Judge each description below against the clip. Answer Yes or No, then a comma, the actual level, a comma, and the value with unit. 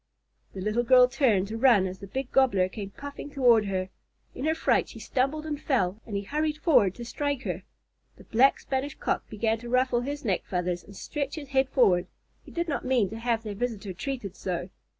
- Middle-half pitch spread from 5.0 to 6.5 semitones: Yes, wide, 5.4 semitones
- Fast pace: Yes, fast, 210 wpm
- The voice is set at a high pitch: Yes, high, 240 Hz